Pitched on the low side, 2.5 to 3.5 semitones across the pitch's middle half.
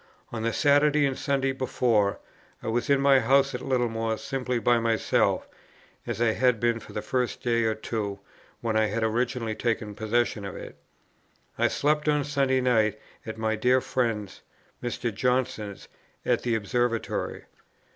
Yes: low, 120 Hz; average, 2.8 semitones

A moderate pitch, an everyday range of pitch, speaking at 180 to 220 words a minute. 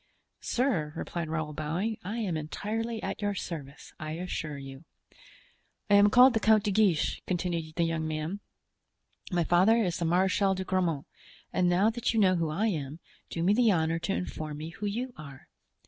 Yes: medium, 180 Hz; average, 4.7 semitones; average, 185 wpm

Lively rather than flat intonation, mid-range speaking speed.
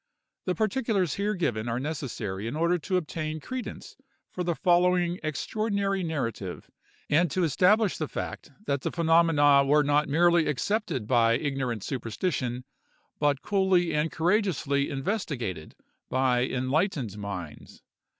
No: wide, 5.8 semitones; slow, 130 wpm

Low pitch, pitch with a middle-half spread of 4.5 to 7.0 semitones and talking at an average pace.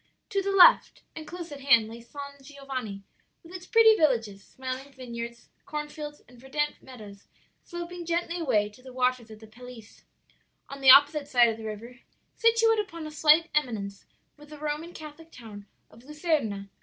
No: very high, 275 Hz; average, 5.1 semitones; average, 170 wpm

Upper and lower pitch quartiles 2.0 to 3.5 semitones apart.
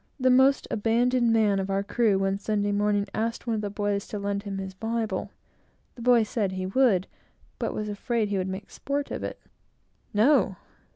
Yes: average, 2.7 semitones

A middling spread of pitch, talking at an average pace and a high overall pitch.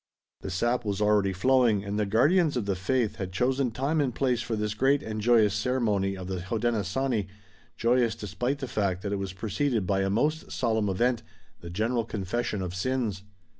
No: average, 4.2 semitones; average, 190 wpm; low, 110 Hz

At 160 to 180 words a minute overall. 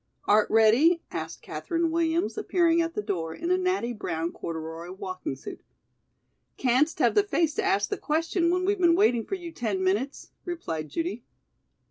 Yes: average, 170 wpm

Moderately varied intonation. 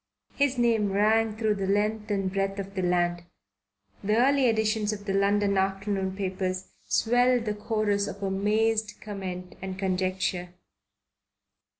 No: narrow, 2.2 semitones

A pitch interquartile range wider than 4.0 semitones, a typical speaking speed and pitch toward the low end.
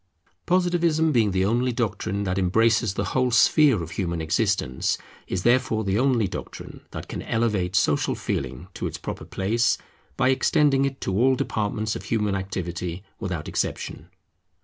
Yes: average, 5.2 semitones; average, 155 wpm; low, 105 Hz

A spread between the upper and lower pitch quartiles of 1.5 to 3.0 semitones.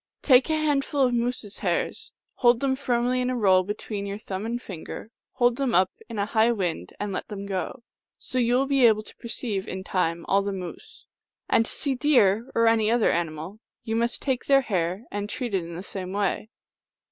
No: average, 4.3 semitones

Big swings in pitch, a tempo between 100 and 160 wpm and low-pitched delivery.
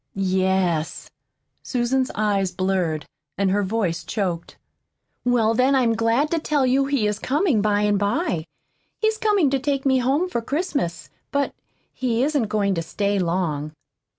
No: wide, 6.2 semitones; average, 150 wpm; high, 225 Hz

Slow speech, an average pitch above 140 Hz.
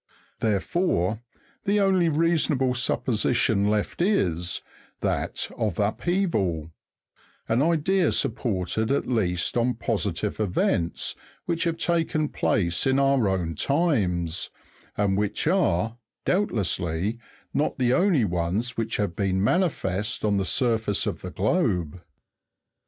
No: slow, 115 wpm; low, 110 Hz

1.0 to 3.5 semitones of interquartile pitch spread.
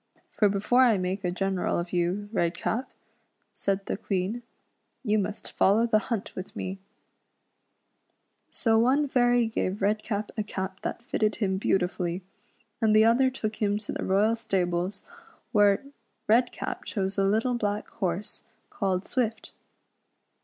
Yes: average, 2.9 semitones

